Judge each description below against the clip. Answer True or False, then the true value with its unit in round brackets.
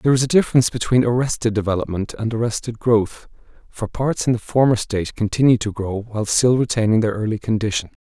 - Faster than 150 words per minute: True (185 wpm)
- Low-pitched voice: True (115 Hz)